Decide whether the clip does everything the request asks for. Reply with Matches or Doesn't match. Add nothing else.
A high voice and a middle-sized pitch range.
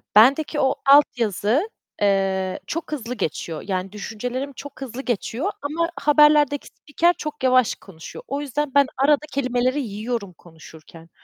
Doesn't match